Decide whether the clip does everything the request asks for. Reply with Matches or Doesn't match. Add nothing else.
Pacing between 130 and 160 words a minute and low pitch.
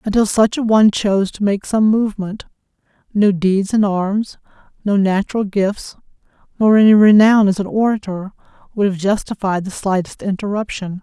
Doesn't match